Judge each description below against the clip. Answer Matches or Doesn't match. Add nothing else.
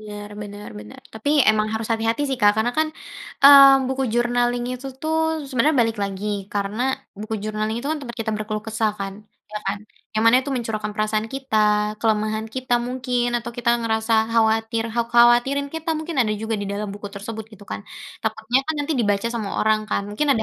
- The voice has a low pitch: Doesn't match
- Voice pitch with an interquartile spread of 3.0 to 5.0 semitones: Doesn't match